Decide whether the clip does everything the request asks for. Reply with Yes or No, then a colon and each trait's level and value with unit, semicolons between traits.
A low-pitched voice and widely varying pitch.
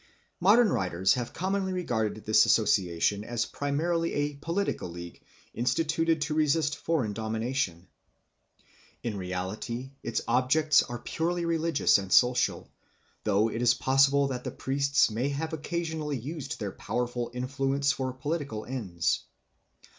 Yes: low, 130 Hz; wide, 6.0 semitones